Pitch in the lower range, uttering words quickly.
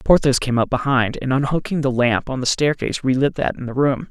Yes: low, 130 Hz; fast, 235 wpm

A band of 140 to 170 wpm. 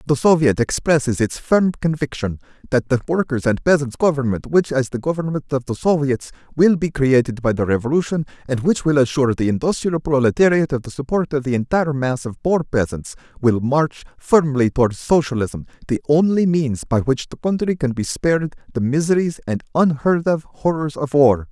No: average, 180 wpm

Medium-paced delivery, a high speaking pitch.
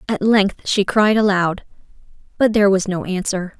Yes: average, 165 wpm; high, 200 Hz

